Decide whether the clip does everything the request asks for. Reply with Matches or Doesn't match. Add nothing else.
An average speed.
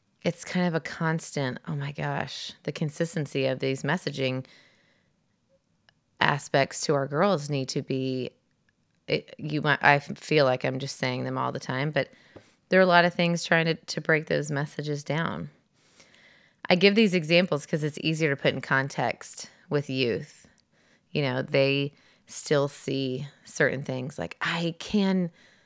Matches